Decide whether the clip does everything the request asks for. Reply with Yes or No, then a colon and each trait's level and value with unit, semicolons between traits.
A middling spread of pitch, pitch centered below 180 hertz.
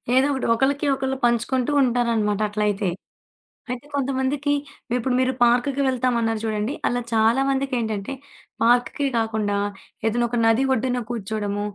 No: average, 3.1 semitones; high, 240 Hz